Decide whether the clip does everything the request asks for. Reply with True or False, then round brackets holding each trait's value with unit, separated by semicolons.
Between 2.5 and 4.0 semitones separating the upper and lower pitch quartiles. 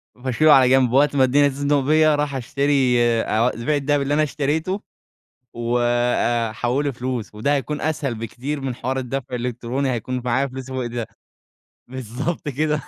True (2.9 semitones)